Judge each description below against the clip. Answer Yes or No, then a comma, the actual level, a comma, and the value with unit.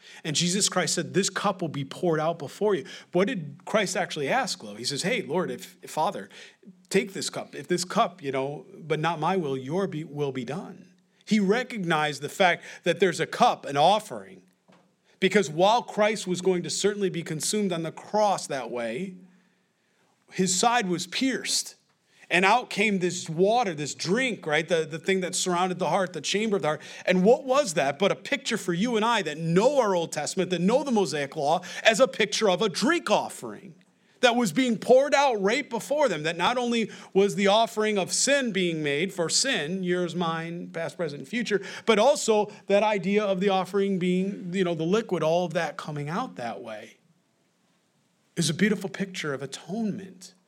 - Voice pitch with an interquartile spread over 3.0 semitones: Yes, average, 3.6 semitones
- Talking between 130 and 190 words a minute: No, average, 200 wpm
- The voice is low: No, high, 190 Hz